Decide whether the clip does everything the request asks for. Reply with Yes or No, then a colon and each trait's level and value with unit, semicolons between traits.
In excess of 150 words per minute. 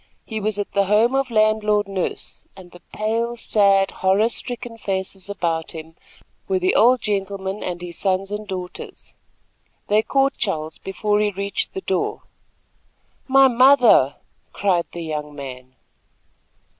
No: average, 145 wpm